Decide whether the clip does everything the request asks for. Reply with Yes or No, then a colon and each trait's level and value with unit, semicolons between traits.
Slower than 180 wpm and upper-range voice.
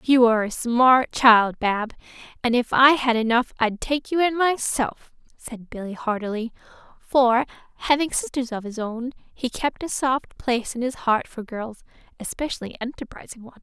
Yes: average, 165 wpm; high, 245 Hz